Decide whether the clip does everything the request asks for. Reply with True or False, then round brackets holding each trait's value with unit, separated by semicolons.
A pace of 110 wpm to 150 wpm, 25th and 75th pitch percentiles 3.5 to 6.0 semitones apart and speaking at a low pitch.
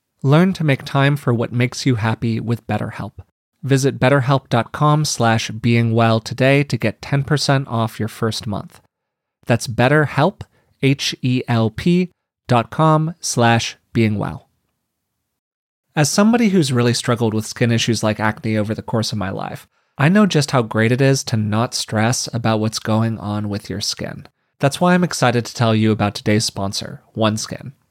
False (160 wpm; 4.0 semitones; 120 Hz)